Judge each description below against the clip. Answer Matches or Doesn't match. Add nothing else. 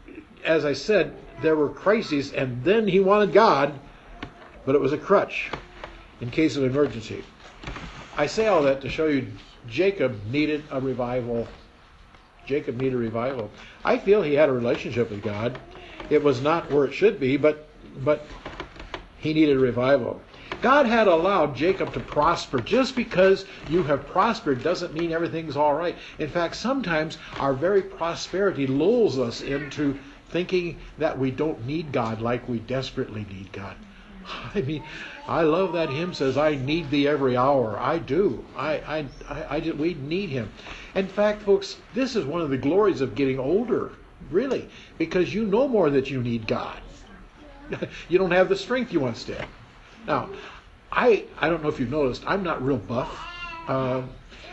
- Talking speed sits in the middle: Matches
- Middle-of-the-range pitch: Matches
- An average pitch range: Matches